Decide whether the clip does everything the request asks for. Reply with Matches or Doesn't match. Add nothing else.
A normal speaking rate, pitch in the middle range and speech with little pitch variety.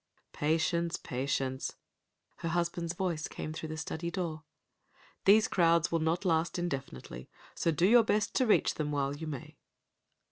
Matches